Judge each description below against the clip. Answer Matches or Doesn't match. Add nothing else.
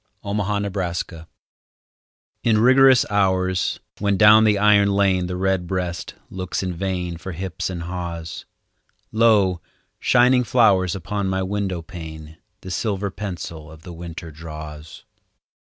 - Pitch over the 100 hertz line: Doesn't match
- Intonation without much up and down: Doesn't match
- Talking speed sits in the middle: Doesn't match